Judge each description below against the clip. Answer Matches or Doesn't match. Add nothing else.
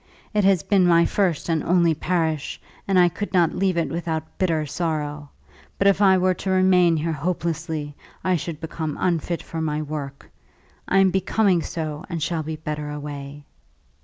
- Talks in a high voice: Doesn't match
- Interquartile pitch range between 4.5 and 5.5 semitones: Doesn't match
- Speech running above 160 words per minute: Matches